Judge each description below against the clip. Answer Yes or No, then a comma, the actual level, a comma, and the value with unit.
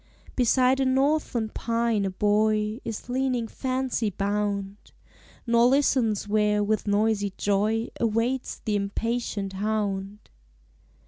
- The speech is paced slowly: Yes, slow, 110 wpm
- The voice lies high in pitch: Yes, high, 220 Hz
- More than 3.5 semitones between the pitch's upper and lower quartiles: No, average, 2.9 semitones